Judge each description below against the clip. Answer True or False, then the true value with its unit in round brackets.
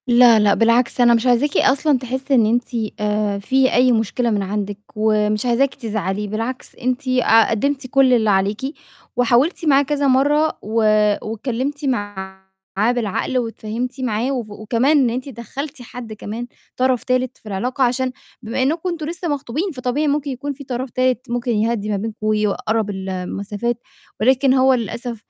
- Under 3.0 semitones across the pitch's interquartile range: False (3.5 semitones)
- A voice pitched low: False (245 Hz)